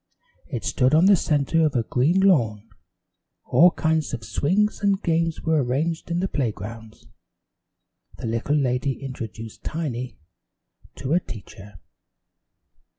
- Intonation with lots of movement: Yes, wide, 6.1 semitones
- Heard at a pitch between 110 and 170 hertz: Yes, medium, 140 Hz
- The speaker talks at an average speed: No, slow, 130 wpm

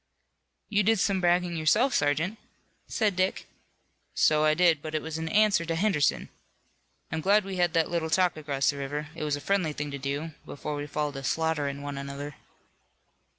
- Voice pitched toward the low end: No, medium, 160 Hz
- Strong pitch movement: No, average, 3.8 semitones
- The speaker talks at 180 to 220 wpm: Yes, average, 190 wpm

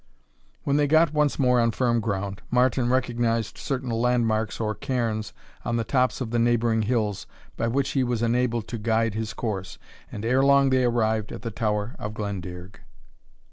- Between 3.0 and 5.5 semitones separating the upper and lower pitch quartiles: No, narrow, 2.6 semitones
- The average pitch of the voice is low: Yes, low, 115 Hz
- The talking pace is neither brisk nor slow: Yes, average, 180 wpm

